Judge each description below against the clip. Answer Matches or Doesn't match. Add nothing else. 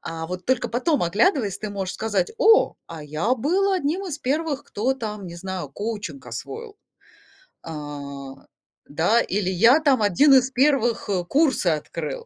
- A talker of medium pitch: Doesn't match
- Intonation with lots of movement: Matches